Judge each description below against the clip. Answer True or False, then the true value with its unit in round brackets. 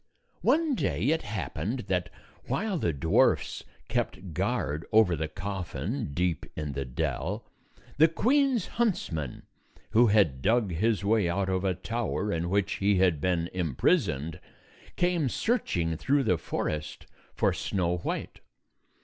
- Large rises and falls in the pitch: True (6.6 semitones)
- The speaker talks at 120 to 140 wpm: True (135 wpm)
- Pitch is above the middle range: False (95 Hz)